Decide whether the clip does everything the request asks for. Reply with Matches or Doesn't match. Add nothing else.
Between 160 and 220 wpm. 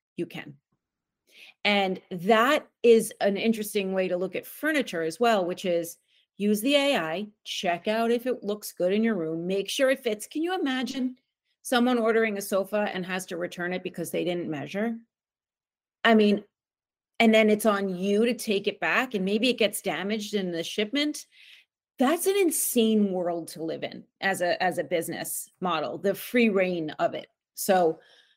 Matches